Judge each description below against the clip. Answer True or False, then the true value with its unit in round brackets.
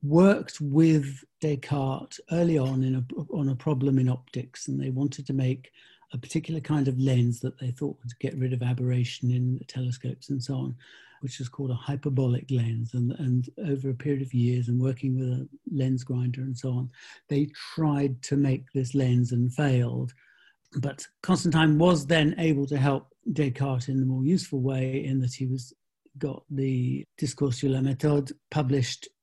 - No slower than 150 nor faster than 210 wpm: True (185 wpm)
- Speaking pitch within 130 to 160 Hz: True (135 Hz)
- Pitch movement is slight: True (2.2 semitones)